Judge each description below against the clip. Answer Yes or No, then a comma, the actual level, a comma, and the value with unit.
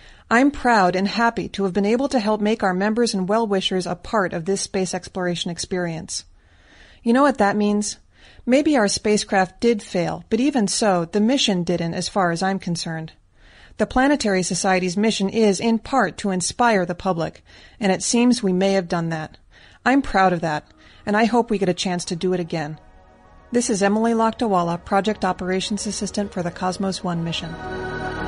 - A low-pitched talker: No, high, 195 Hz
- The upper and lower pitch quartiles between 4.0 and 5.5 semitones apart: No, average, 3.6 semitones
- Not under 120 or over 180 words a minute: No, average, 190 wpm